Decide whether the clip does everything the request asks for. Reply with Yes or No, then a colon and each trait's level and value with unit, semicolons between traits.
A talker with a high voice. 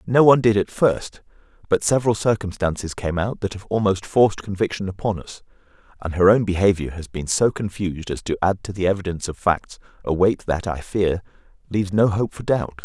No: very low, 95 Hz